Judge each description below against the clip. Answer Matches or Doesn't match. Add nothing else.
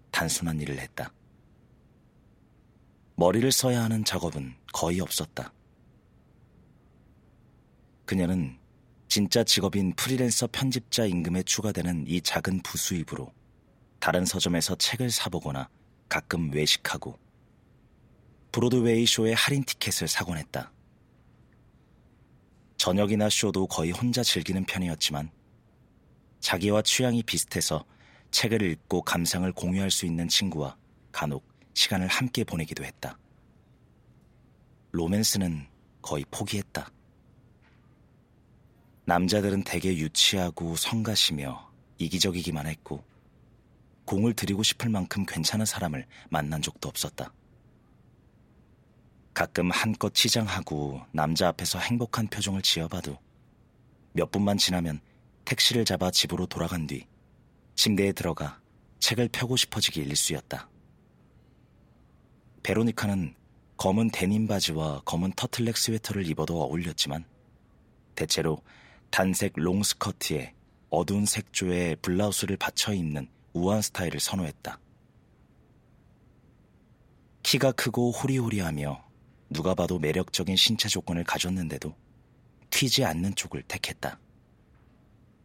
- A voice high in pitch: Doesn't match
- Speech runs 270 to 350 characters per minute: Doesn't match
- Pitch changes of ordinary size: Matches